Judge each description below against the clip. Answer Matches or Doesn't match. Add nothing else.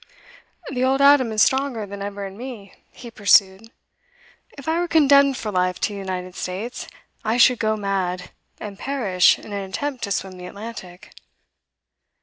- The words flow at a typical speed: Matches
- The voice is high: Matches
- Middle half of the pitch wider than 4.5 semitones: Matches